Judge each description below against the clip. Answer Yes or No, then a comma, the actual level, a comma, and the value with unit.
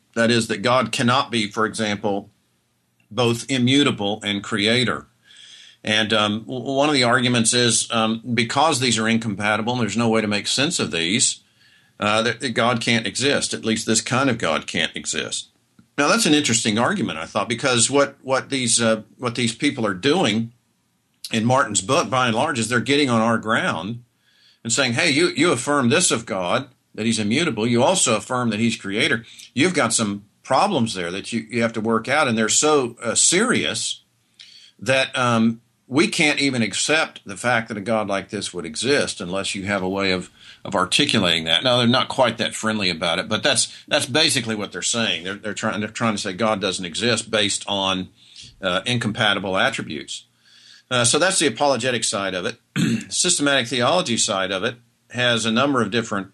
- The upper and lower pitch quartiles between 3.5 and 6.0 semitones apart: No, narrow, 2.6 semitones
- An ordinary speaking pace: Yes, average, 195 wpm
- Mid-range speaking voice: No, low, 115 Hz